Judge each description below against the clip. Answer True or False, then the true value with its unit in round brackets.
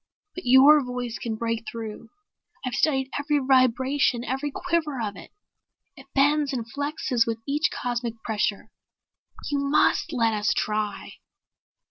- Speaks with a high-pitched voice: True (255 Hz)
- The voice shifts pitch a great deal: False (3.8 semitones)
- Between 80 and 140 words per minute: True (135 wpm)